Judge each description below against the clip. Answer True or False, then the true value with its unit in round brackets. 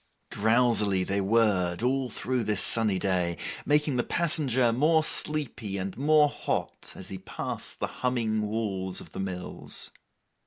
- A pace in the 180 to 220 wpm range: False (145 wpm)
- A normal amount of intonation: True (5.0 semitones)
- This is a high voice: False (110 Hz)